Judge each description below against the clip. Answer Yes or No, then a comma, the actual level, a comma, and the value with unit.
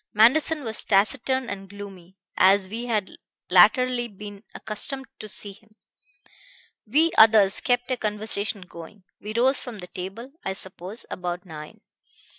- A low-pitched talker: No, high, 210 Hz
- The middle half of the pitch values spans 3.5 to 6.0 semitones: Yes, average, 3.9 semitones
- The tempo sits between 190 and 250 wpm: No, average, 140 wpm